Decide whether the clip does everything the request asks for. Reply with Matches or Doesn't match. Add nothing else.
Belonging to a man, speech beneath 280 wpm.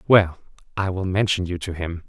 Matches